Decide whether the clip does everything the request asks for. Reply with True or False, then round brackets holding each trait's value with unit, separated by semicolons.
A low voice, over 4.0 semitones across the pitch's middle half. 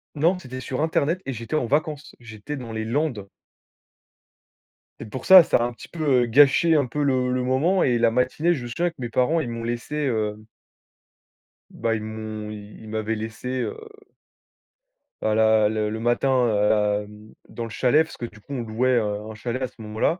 True (120 Hz; 4.4 semitones)